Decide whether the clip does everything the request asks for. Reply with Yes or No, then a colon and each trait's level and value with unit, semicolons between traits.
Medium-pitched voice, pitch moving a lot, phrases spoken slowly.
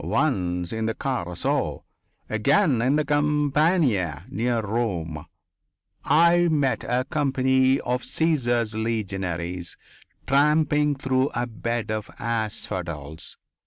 No: low, 120 Hz; wide, 6.6 semitones; slow, 100 wpm